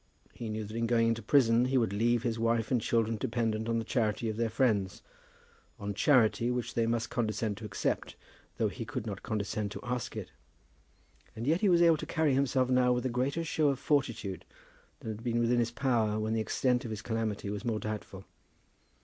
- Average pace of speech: No, fast, 210 wpm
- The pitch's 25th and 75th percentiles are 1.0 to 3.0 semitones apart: Yes, narrow, 2.5 semitones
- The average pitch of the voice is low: Yes, low, 115 Hz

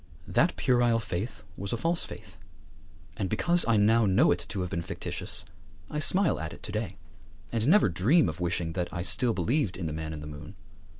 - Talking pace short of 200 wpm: No, fast, 205 wpm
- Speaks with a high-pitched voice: No, low, 100 Hz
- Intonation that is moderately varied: No, wide, 5.8 semitones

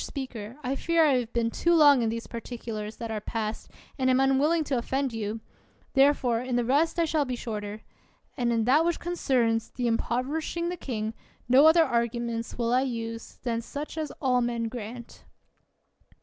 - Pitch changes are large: No, average, 3.6 semitones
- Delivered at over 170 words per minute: Yes, average, 185 wpm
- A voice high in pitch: Yes, high, 245 Hz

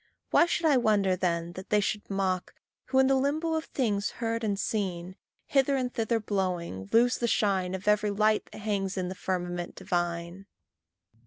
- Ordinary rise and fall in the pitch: Yes, average, 4.1 semitones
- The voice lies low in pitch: No, high, 205 Hz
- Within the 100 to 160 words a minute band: No, average, 180 wpm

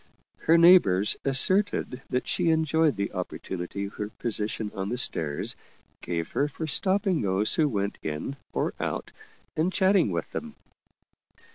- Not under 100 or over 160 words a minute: Yes, average, 145 wpm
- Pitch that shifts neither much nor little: No, wide, 8.6 semitones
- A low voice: Yes, low, 125 Hz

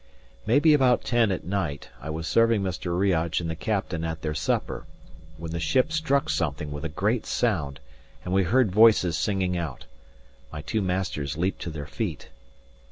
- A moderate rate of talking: Yes, average, 175 wpm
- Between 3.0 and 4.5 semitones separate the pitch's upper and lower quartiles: No, wide, 5.4 semitones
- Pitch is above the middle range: No, very low, 90 Hz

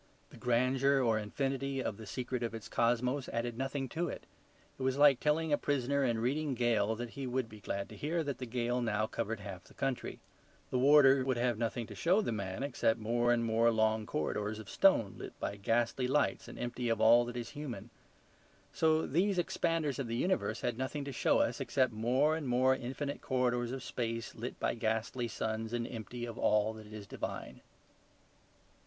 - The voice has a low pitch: Yes, low, 120 Hz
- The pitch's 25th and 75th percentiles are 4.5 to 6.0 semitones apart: No, average, 3.2 semitones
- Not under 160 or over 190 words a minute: No, average, 200 wpm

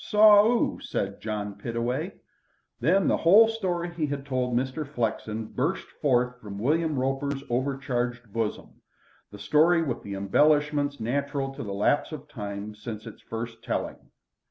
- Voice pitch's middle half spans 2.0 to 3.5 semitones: No, average, 4.9 semitones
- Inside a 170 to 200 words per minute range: No, average, 150 wpm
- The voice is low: Yes, low, 130 Hz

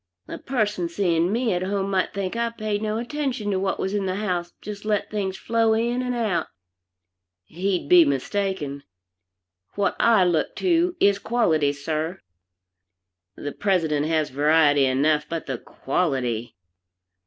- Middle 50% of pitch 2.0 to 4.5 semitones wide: No, wide, 5.4 semitones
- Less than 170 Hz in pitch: No, high, 190 Hz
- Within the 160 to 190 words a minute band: No, average, 150 wpm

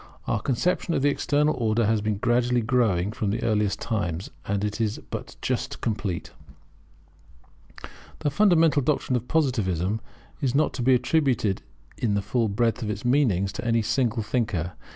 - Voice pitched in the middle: No, low, 115 Hz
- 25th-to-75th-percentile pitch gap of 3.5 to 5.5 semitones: Yes, average, 3.8 semitones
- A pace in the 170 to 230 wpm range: No, average, 160 wpm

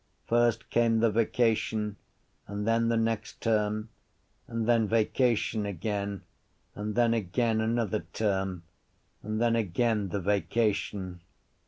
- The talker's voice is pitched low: Yes, low, 110 Hz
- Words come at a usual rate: No, slow, 120 wpm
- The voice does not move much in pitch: Yes, narrow, 2.0 semitones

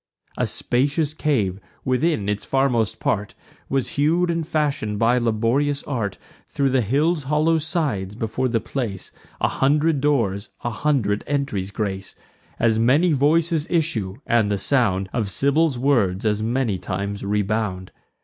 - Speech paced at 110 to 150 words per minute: Yes, average, 140 wpm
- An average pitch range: No, wide, 5.9 semitones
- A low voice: Yes, low, 125 Hz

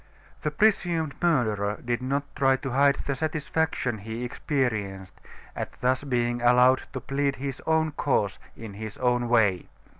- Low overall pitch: Yes, low, 130 Hz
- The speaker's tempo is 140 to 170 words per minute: Yes, average, 150 wpm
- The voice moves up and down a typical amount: Yes, average, 3.6 semitones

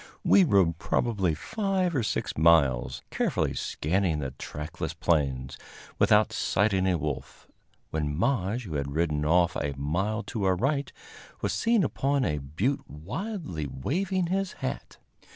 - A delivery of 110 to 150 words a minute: Yes, average, 140 wpm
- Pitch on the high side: No, very low, 90 Hz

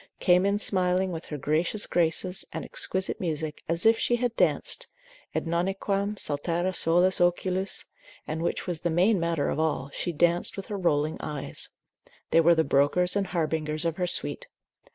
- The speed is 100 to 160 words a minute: No, average, 175 wpm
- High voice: No, medium, 175 Hz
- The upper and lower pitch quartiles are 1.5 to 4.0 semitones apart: Yes, average, 2.8 semitones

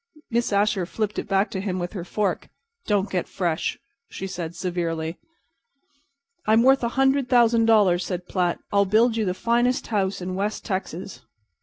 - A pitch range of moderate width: Yes, average, 3.9 semitones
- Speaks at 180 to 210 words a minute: No, average, 170 wpm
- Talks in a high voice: Yes, high, 200 Hz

